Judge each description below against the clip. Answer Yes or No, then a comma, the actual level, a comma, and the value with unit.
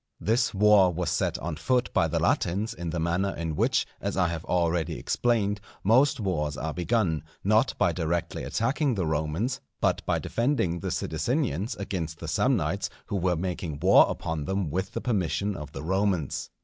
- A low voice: Yes, very low, 90 Hz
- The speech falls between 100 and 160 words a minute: No, average, 175 wpm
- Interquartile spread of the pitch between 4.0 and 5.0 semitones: Yes, average, 4.3 semitones